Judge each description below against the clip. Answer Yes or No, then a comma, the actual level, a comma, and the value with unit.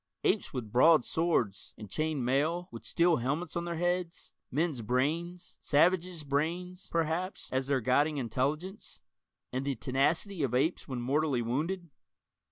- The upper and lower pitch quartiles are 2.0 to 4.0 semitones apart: No, average, 4.8 semitones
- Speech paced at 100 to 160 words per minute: Yes, average, 140 wpm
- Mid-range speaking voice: Yes, medium, 155 Hz